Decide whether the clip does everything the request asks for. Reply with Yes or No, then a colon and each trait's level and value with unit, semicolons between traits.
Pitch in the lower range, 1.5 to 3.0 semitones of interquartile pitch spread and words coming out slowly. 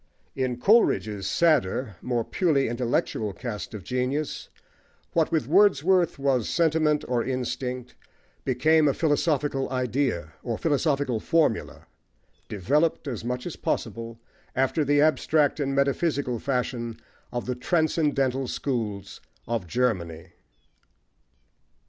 No: low, 130 Hz; average, 4.2 semitones; slow, 110 wpm